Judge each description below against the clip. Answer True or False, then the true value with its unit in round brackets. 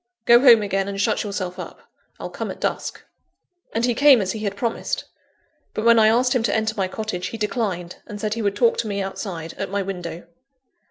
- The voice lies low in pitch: False (210 Hz)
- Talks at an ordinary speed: False (220 wpm)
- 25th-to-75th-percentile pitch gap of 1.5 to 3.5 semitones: True (2.8 semitones)